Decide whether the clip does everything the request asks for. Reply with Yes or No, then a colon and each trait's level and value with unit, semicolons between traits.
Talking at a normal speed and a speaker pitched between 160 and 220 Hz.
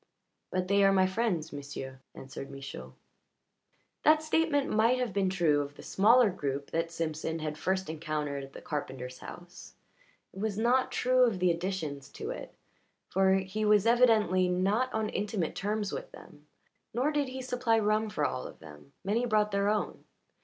Yes: average, 175 wpm; high, 190 Hz